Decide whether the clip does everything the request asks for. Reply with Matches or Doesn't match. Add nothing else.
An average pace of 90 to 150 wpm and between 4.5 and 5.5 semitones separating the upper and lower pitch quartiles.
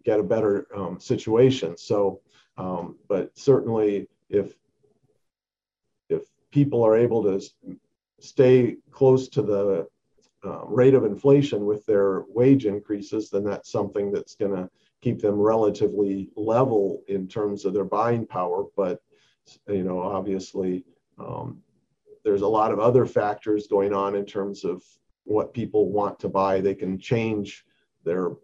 Matches